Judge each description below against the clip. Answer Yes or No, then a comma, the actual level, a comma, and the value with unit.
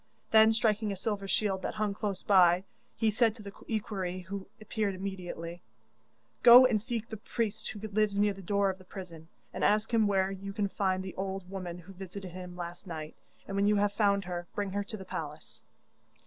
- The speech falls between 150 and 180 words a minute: No, fast, 205 wpm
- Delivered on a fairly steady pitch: Yes, narrow, 2.2 semitones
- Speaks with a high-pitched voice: Yes, high, 200 Hz